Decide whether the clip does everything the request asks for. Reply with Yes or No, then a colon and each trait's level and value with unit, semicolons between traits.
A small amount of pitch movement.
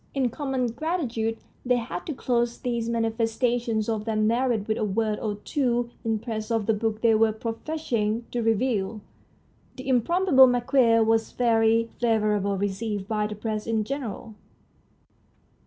Yes: narrow, 2.1 semitones